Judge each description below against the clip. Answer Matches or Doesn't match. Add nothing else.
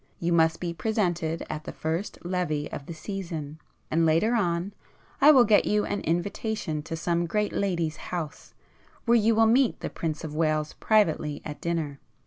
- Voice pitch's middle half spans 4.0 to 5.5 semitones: Matches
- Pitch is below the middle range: Doesn't match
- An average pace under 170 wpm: Doesn't match